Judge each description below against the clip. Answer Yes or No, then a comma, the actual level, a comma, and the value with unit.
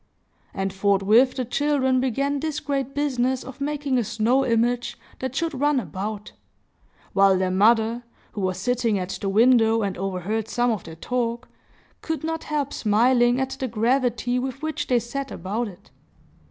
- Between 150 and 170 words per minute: Yes, average, 165 wpm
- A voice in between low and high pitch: No, high, 240 Hz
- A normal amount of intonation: Yes, average, 4.1 semitones